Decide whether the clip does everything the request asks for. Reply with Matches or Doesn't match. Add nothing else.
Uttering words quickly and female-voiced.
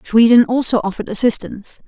Doesn't match